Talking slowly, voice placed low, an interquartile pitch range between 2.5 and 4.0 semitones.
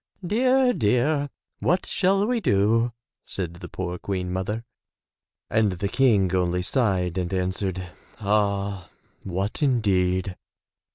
No: slow, 115 wpm; low, 100 Hz; average, 5.3 semitones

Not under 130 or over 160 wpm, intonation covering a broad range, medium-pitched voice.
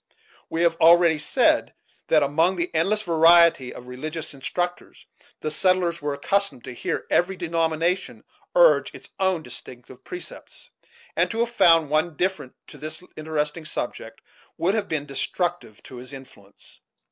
No: average, 145 wpm; average, 3.4 semitones; medium, 165 Hz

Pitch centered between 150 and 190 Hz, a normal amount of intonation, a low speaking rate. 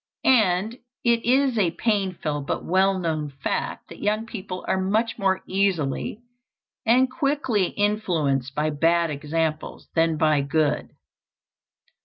No: medium, 185 Hz; wide, 5.8 semitones; slow, 125 wpm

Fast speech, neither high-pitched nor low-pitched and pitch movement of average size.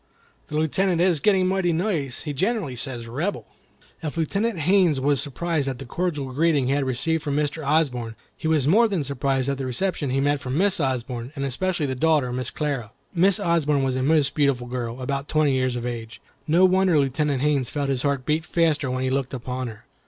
Yes: fast, 210 wpm; medium, 145 Hz; average, 4.0 semitones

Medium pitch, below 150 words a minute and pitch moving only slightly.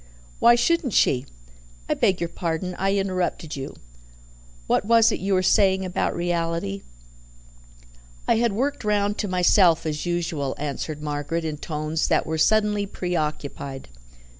No: medium, 175 Hz; average, 140 wpm; average, 4.6 semitones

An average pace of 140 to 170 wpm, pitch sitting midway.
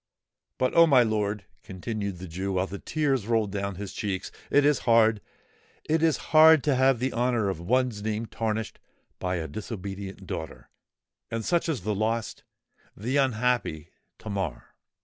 No: average, 145 wpm; low, 110 Hz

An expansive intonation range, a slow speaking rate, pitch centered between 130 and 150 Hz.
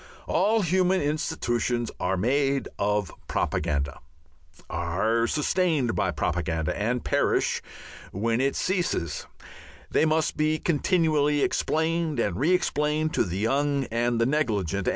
Yes: wide, 7.2 semitones; slow, 120 wpm; low, 135 Hz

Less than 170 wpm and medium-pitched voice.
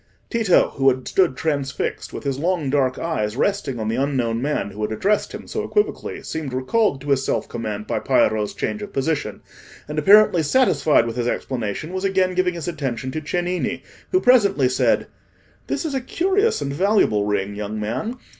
No: average, 185 wpm; medium, 145 Hz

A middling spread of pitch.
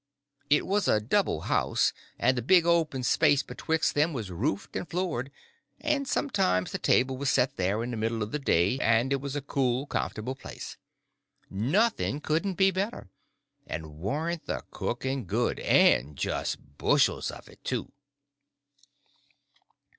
No: wide, 6.8 semitones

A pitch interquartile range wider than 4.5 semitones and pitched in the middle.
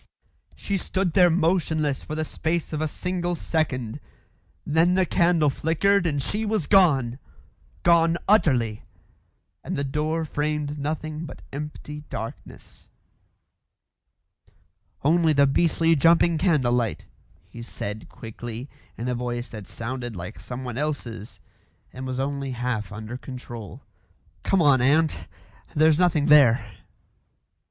Yes: average, 5.0 semitones; medium, 150 Hz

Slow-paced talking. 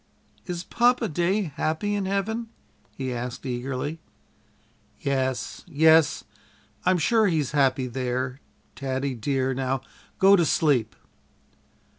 Yes: slow, 110 wpm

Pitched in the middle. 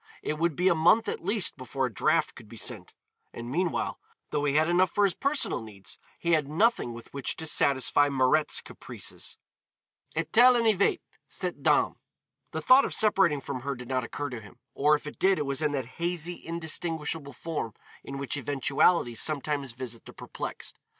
Yes: medium, 150 Hz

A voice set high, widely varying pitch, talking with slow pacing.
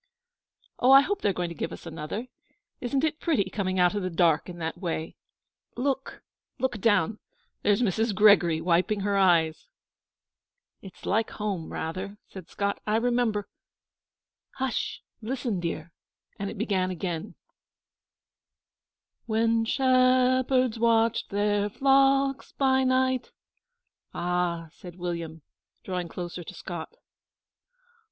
Yes: high, 205 Hz; wide, 5.7 semitones; slow, 130 wpm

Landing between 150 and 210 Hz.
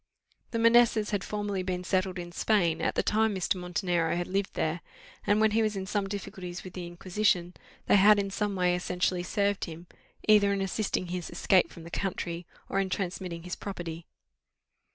Yes: medium, 185 Hz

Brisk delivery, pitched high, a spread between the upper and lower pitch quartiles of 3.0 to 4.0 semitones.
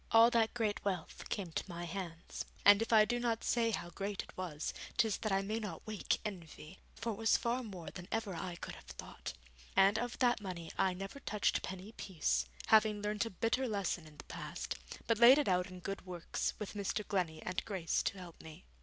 Yes: fast, 215 wpm; high, 200 Hz; average, 3.7 semitones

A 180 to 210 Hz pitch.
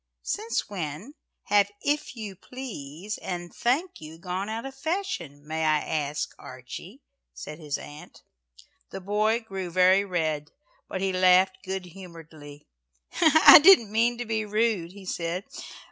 Yes: high, 190 Hz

